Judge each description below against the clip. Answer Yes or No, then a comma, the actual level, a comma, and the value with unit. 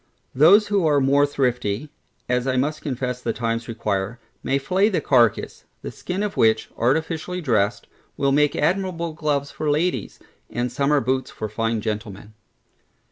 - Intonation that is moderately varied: Yes, average, 5.0 semitones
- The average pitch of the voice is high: No, low, 135 Hz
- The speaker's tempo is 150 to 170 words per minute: Yes, average, 155 wpm